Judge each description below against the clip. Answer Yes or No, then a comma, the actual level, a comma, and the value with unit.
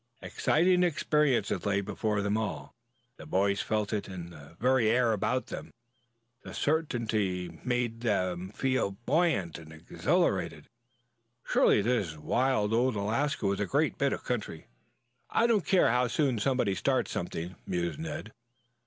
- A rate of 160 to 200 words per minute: No, average, 145 wpm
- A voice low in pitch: Yes, low, 110 Hz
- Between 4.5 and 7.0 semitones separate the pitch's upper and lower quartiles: Yes, average, 5.1 semitones